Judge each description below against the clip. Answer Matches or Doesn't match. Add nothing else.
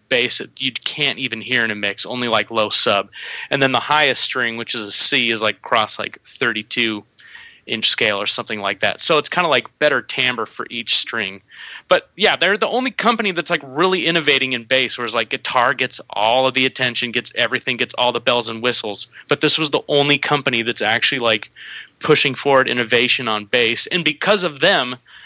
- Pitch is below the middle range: Matches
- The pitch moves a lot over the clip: Doesn't match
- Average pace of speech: Doesn't match